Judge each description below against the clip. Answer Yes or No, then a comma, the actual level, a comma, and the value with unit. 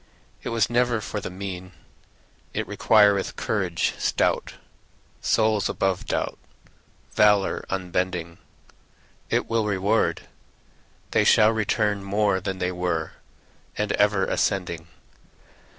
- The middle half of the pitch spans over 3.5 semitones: No, narrow, 2.6 semitones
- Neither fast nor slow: No, slow, 105 wpm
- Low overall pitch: Yes, low, 100 Hz